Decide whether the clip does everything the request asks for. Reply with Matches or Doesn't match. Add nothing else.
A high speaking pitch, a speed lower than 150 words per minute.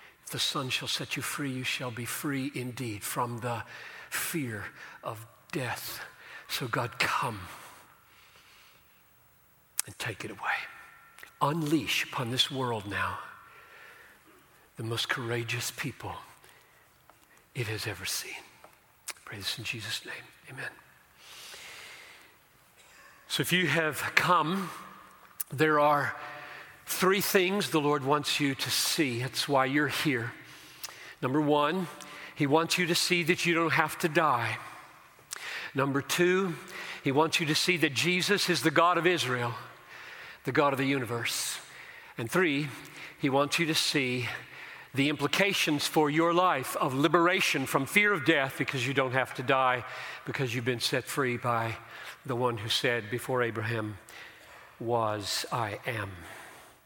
Doesn't match